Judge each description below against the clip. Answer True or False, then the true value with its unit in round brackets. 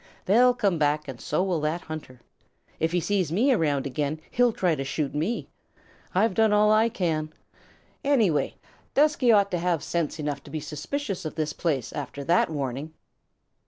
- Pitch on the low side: False (165 Hz)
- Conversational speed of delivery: True (180 wpm)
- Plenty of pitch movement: True (5.7 semitones)